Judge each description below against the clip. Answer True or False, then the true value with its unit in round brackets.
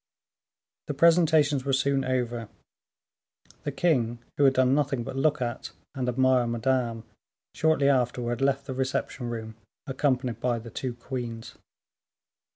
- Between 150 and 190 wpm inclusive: False (135 wpm)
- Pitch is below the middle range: True (130 Hz)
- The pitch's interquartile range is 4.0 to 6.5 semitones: False (2.6 semitones)